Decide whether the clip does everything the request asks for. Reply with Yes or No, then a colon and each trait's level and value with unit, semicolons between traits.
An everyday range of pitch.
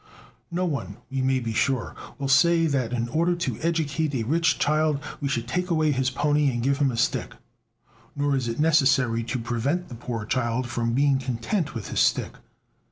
Yes: average, 4.5 semitones